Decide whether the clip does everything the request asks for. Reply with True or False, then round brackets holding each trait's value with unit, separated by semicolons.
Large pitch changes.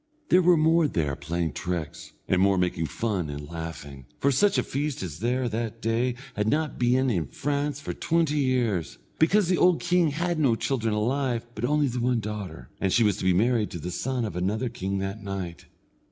True (7.4 semitones)